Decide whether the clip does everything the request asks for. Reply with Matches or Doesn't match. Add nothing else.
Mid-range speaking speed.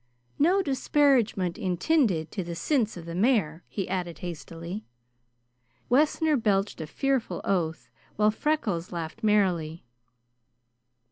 Doesn't match